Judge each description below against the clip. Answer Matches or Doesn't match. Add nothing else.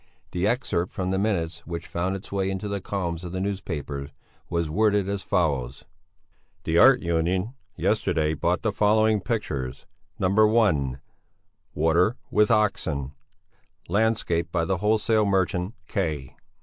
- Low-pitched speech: Matches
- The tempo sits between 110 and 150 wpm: Matches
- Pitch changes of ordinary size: Matches